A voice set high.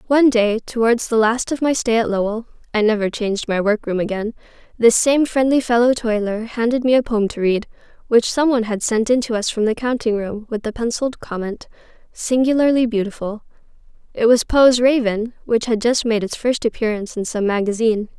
Yes: high, 230 Hz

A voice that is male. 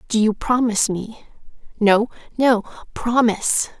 No: female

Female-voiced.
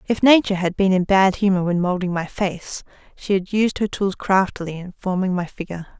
Yes: female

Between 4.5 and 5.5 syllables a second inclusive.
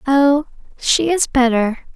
No: 3.7 syllables/s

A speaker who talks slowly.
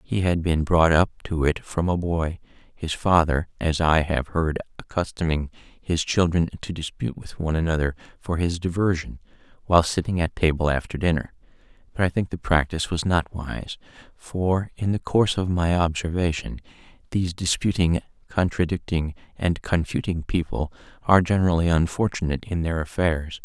No: average, 155 wpm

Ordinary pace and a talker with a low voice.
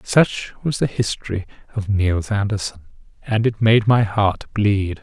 Yes: average, 155 wpm; low, 105 Hz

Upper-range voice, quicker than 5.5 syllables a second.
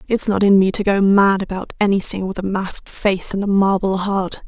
No: high, 195 Hz; 5.2 syllables/s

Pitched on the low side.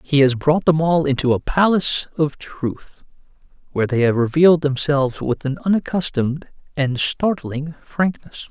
No: medium, 145 Hz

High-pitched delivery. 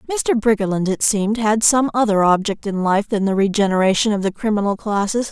Yes: high, 210 Hz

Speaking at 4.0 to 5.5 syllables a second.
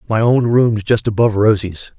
Yes: 5.1 syllables/s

